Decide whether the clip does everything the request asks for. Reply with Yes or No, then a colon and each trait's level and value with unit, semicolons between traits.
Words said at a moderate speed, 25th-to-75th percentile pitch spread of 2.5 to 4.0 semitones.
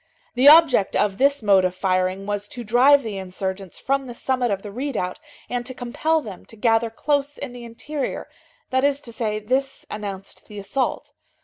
No: average, 190 wpm; average, 5.1 semitones